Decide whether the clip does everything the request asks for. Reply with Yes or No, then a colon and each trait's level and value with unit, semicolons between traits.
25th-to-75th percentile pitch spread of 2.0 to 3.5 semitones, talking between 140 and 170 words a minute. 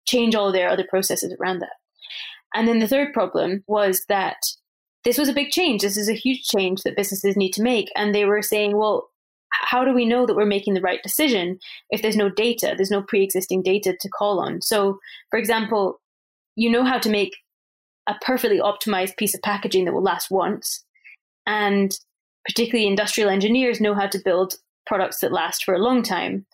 No: average, 3.2 semitones; average, 200 wpm